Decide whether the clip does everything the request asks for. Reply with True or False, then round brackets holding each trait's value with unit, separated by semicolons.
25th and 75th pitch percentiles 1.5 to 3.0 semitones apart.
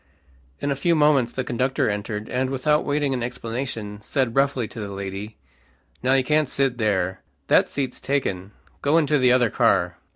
False (4.5 semitones)